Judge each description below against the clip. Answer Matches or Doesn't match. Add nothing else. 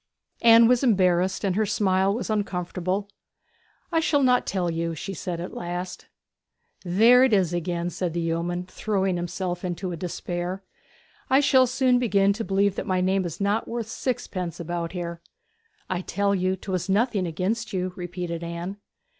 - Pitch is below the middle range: Doesn't match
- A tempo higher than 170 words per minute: Doesn't match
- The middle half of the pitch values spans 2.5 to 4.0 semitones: Matches